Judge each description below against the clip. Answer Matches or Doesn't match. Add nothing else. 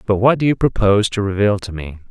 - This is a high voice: Doesn't match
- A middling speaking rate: Doesn't match